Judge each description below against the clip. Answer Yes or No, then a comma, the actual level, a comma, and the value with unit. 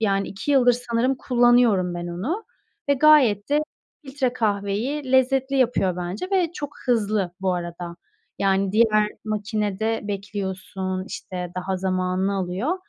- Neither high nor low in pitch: No, high, 210 Hz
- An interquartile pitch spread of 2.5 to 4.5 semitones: No, average, 5.1 semitones